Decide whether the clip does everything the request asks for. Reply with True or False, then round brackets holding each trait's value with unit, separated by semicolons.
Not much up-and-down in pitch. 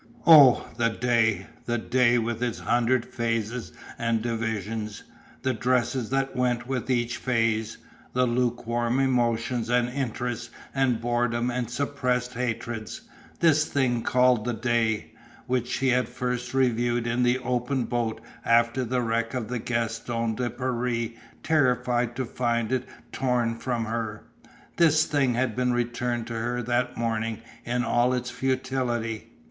True (1.5 semitones)